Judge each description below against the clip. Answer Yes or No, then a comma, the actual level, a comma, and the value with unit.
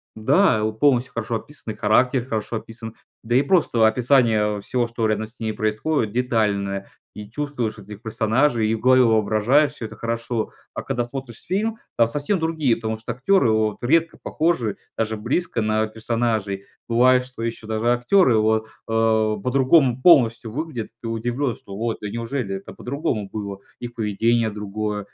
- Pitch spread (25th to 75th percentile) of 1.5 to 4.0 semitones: Yes, average, 2.9 semitones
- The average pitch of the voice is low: Yes, low, 115 Hz